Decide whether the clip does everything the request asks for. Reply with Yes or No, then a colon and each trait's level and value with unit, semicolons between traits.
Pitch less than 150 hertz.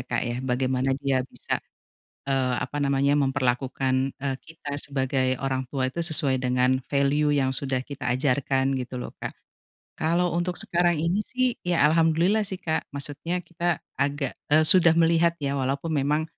Yes: medium, 140 Hz